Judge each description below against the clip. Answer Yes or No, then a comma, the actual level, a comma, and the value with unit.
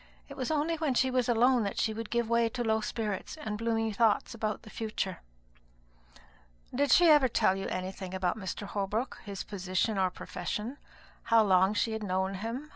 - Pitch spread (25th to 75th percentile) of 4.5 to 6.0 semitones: No, average, 3.7 semitones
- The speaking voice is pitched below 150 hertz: No, high, 220 Hz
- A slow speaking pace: No, average, 190 wpm